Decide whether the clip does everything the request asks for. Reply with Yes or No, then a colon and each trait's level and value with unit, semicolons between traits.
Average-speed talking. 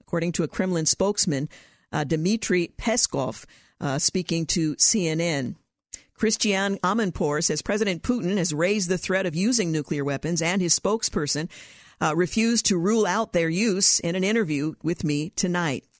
Yes: average, 155 wpm